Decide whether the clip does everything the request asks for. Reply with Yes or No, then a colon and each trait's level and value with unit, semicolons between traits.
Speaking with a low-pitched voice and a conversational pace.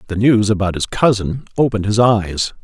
Yes: low, 105 Hz; average, 180 wpm